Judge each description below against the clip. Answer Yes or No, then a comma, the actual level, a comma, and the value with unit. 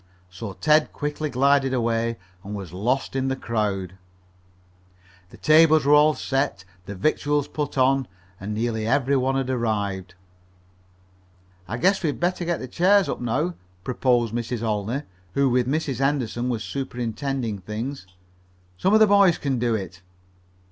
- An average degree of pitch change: Yes, average, 4.6 semitones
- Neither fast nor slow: Yes, average, 150 wpm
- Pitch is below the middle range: Yes, low, 130 Hz